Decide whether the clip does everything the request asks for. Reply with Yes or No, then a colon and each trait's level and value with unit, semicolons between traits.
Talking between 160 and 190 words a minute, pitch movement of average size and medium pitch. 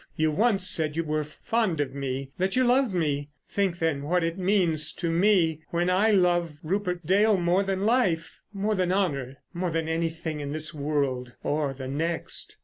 Yes: average, 175 wpm; average, 3.9 semitones; medium, 170 Hz